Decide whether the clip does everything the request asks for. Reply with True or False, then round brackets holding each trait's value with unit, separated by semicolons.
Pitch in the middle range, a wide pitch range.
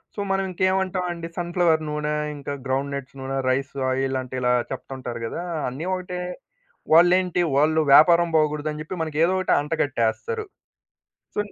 False (155 Hz; 4.6 semitones)